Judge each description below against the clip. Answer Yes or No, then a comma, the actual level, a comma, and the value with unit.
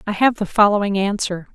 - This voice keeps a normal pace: Yes, average, 195 wpm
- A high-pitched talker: Yes, high, 205 Hz